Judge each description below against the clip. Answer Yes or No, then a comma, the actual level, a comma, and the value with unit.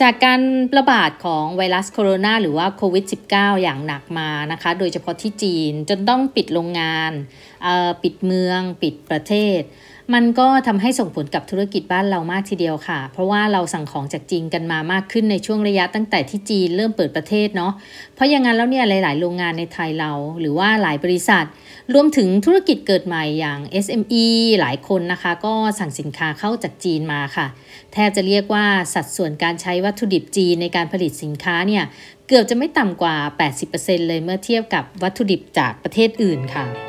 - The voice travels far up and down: No, average, 4.3 semitones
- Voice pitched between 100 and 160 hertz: No, medium, 185 Hz